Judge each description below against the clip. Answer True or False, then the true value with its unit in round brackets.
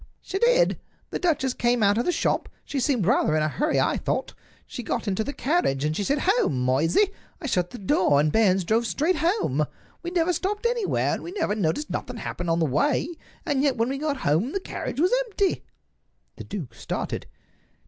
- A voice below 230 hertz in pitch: False (250 Hz)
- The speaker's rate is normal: False (210 wpm)